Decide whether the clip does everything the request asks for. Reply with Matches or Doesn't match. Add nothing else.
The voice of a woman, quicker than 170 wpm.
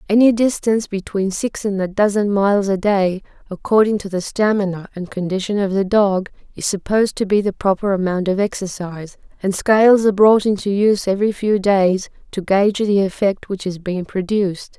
Matches